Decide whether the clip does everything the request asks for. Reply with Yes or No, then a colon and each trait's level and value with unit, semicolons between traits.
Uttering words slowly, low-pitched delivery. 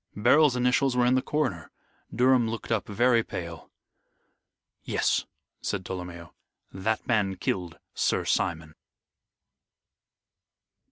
Yes: slow, 105 wpm; low, 110 Hz